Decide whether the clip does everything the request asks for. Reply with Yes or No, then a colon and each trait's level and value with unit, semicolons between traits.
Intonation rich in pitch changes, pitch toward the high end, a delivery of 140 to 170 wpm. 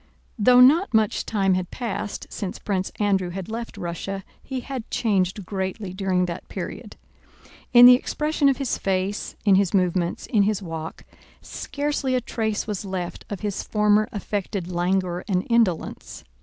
No: average, 3.7 semitones; high, 200 Hz; average, 155 wpm